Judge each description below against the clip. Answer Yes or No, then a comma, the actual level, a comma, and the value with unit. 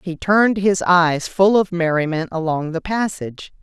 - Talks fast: No, average, 165 wpm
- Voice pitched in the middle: Yes, medium, 175 Hz